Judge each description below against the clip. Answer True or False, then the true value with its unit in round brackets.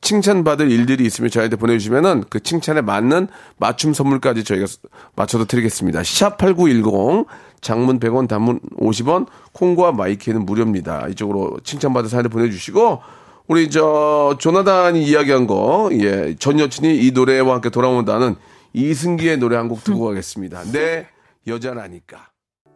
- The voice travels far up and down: True (5.7 semitones)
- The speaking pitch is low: True (120 Hz)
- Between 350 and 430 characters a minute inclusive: False (335 characters per minute)